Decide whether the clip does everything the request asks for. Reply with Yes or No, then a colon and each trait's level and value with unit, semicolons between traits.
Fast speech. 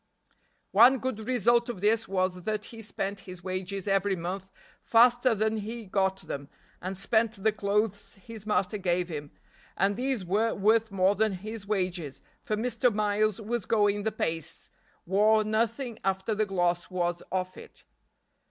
No: average, 160 wpm